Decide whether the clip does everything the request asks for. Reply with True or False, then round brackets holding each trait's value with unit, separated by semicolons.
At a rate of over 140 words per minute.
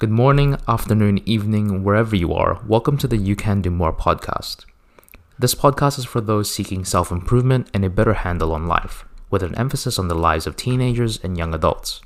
True (200 wpm)